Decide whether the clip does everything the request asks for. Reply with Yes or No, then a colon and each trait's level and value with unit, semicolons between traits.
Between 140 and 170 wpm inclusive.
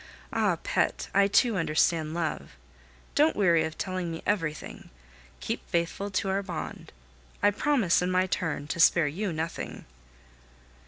Yes: average, 145 wpm